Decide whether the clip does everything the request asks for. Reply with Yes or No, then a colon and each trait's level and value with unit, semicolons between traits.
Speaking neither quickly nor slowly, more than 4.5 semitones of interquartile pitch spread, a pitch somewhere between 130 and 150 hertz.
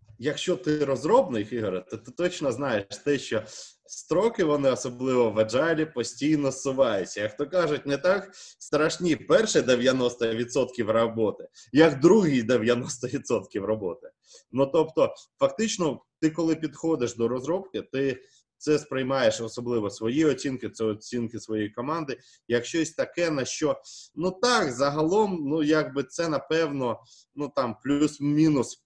Yes: average, 130 wpm; average, 4.9 semitones; medium, 140 Hz